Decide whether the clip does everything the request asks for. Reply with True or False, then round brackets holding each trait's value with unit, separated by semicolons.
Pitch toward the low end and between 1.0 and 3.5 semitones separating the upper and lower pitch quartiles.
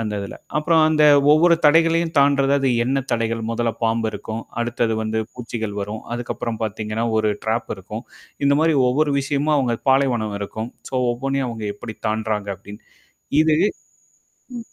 False (120 Hz; 4.2 semitones)